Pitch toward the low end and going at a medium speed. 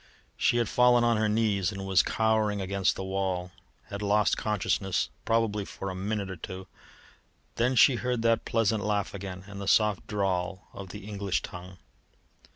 Yes: low, 100 Hz; average, 170 wpm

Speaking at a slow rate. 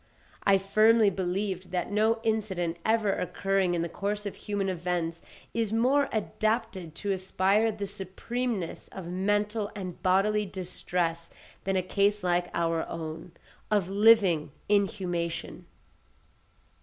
Yes: slow, 125 wpm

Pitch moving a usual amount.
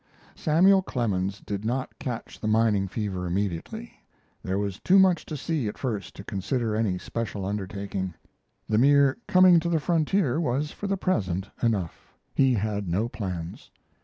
No: wide, 6.6 semitones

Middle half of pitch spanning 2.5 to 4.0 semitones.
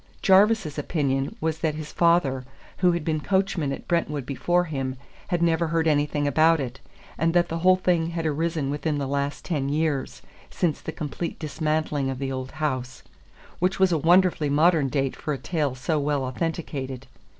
Yes: average, 3.2 semitones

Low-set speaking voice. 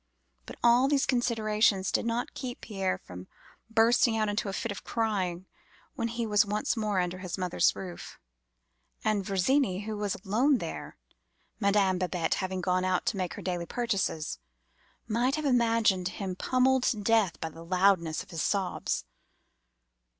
No: high, 205 Hz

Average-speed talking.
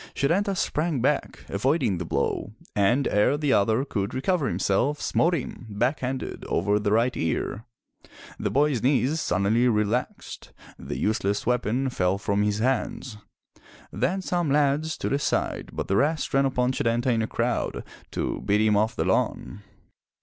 Yes: average, 155 wpm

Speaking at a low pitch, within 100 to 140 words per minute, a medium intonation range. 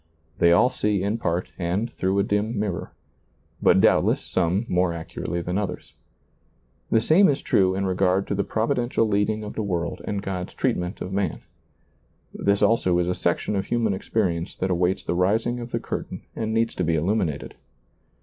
No: low, 100 Hz; average, 180 wpm; average, 3.5 semitones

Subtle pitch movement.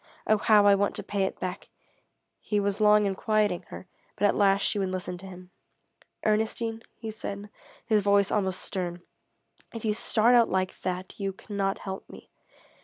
Yes: narrow, 2.0 semitones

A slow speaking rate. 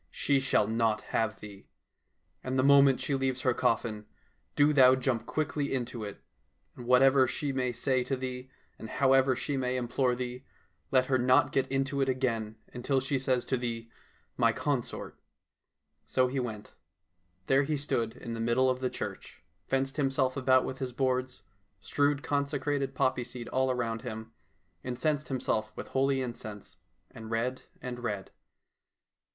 No: average, 170 wpm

